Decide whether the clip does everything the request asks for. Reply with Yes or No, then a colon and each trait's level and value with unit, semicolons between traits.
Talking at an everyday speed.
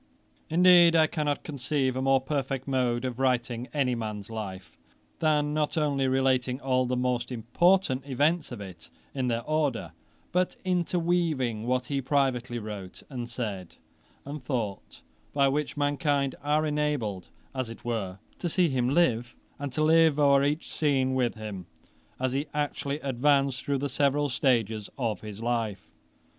Yes: average, 155 wpm